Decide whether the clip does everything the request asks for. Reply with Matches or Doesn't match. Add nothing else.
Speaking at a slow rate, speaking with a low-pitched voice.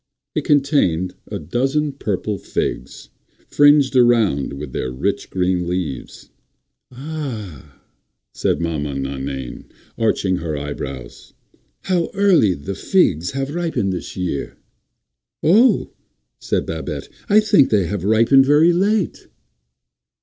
Matches